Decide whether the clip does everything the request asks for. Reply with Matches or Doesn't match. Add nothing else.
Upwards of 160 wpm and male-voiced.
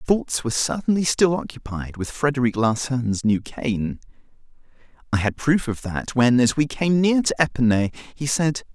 Matches